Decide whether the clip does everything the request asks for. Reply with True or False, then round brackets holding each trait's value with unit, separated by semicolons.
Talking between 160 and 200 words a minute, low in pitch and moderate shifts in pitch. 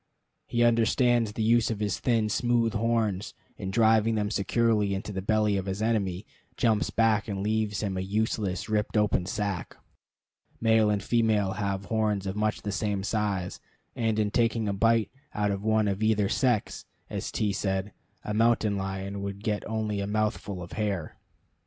False (175 wpm; 105 Hz; 2.0 semitones)